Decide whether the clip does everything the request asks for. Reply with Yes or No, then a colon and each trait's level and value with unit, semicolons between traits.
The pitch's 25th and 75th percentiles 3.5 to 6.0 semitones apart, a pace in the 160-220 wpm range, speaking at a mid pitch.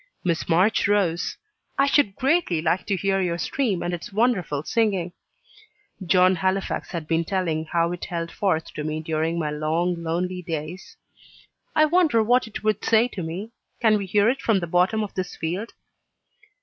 Yes: average, 4.2 semitones; average, 175 wpm; medium, 180 Hz